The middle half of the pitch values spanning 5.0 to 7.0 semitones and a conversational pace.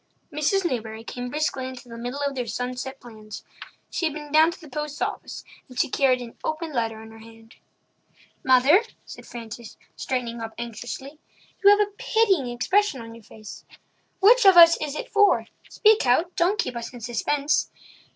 Yes: wide, 5.5 semitones; average, 175 wpm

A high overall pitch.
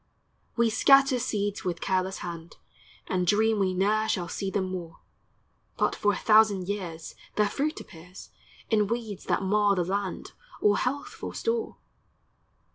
Yes: high, 205 Hz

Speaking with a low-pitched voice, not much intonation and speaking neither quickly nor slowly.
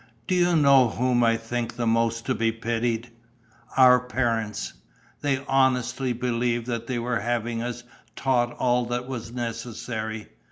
Yes: low, 120 Hz; narrow, 1.5 semitones; average, 150 wpm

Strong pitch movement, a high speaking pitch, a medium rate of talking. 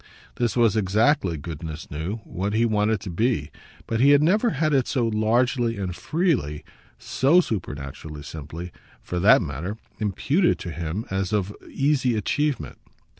No: wide, 6.9 semitones; low, 105 Hz; average, 150 wpm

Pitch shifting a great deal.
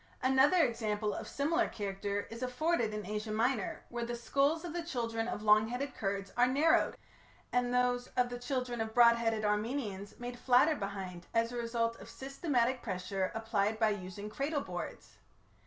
No: average, 3.2 semitones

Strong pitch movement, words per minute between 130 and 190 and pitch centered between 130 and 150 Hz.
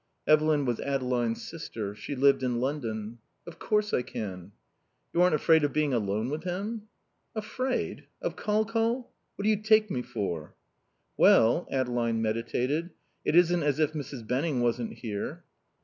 Yes: wide, 7.1 semitones; average, 160 wpm; medium, 140 Hz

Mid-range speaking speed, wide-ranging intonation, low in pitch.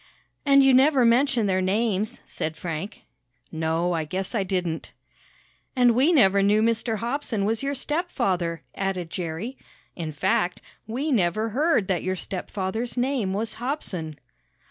No: average, 145 wpm; wide, 5.7 semitones; high, 210 Hz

